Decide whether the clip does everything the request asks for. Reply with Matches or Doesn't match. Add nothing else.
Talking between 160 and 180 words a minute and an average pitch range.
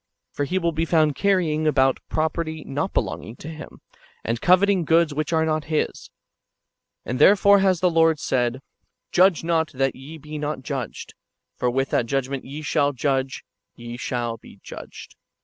Matches